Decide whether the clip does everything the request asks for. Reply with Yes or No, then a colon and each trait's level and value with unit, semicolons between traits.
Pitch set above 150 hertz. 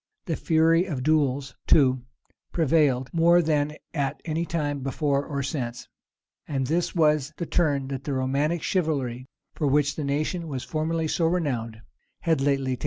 No: medium, 145 Hz